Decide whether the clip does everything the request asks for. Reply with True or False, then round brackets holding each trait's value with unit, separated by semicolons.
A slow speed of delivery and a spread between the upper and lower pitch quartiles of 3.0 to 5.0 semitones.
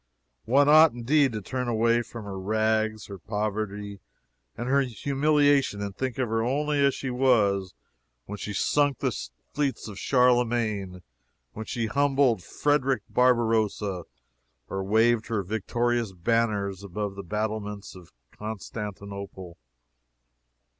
True (125 wpm; 3.9 semitones)